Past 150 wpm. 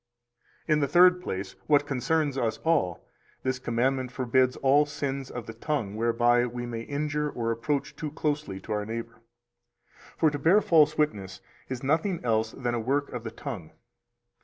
Yes: average, 175 wpm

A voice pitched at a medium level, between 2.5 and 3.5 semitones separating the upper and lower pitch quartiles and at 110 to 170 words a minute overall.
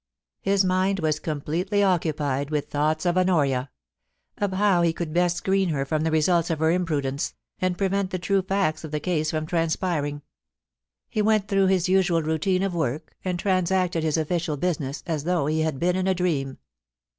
No: medium, 170 Hz; average, 3.2 semitones; average, 190 wpm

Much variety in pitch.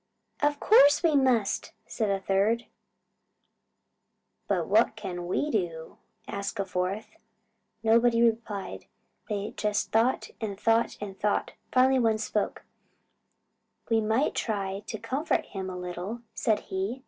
No: average, 3.3 semitones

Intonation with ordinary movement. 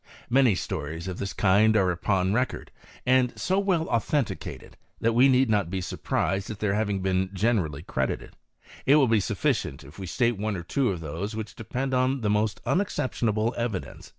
Yes: average, 4.9 semitones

